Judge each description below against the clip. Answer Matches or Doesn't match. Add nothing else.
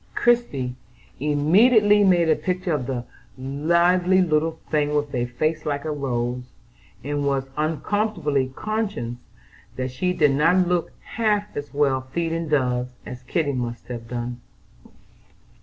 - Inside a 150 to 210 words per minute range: Doesn't match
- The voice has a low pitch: Doesn't match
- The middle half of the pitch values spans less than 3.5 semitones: Doesn't match